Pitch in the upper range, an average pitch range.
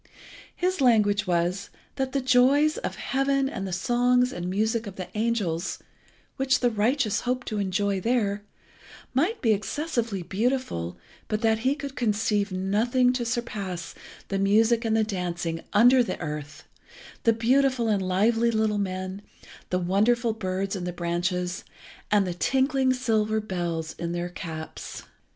Yes: high, 215 Hz; average, 4.9 semitones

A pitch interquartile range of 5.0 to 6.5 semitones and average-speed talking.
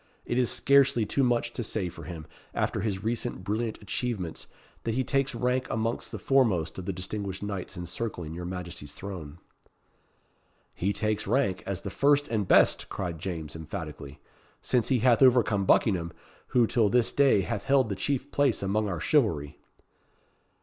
Yes: wide, 5.4 semitones; average, 165 wpm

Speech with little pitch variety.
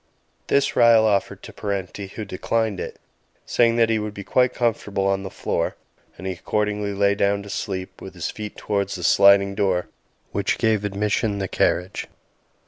Yes: narrow, 1.7 semitones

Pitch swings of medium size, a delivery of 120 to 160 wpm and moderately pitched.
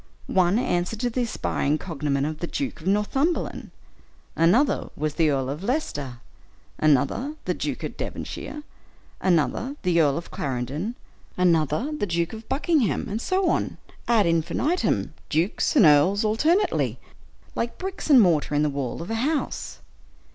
No: wide, 8.6 semitones; average, 150 wpm; medium, 180 Hz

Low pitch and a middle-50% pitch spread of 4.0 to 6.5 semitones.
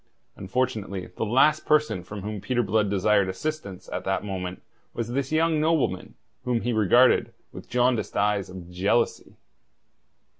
Yes: low, 110 Hz; average, 4.8 semitones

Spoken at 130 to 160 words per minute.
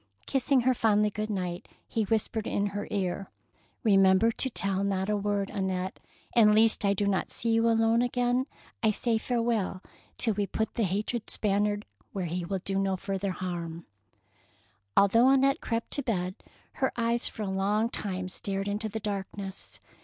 No: average, 180 wpm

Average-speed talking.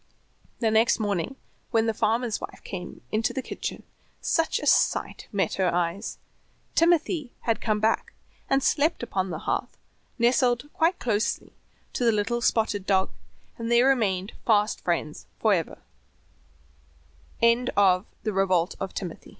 No: slow, 130 wpm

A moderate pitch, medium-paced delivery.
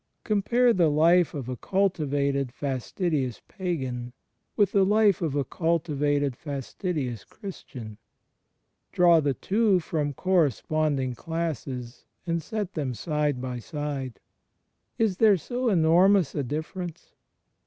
No: medium, 155 Hz; slow, 115 wpm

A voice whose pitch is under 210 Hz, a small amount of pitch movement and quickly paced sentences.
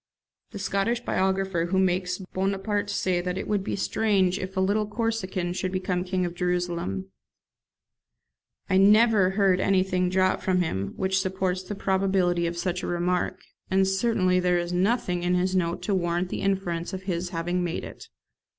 No: medium, 185 Hz; narrow, 1.5 semitones; average, 170 wpm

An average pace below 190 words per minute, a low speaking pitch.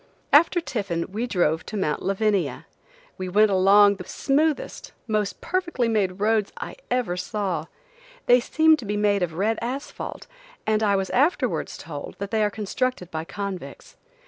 No: average, 160 wpm; high, 210 Hz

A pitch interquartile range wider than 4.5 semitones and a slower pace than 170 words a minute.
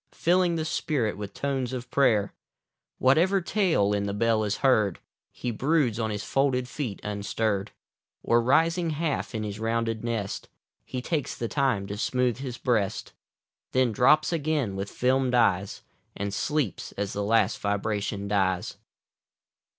Yes: average, 5.1 semitones; average, 150 wpm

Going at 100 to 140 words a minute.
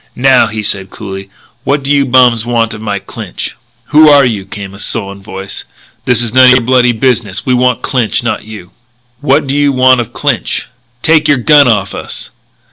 No: average, 200 wpm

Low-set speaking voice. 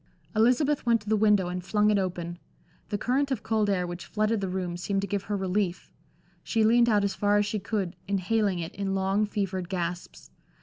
No: high, 200 Hz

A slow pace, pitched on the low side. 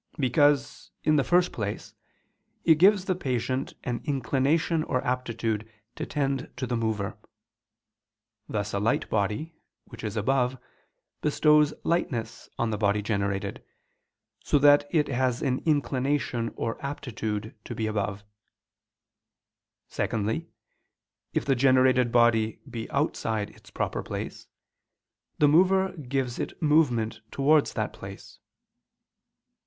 Yes: slow, 120 wpm; low, 130 Hz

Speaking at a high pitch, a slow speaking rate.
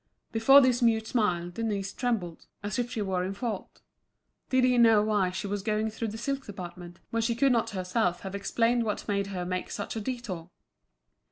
No: high, 215 Hz; average, 195 wpm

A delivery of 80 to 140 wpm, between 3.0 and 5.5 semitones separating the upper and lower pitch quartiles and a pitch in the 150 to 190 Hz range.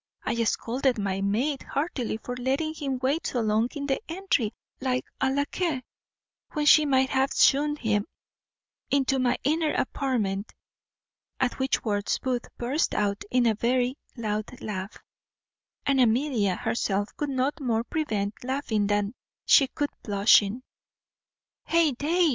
No: slow, 135 wpm; average, 4.5 semitones; very high, 255 Hz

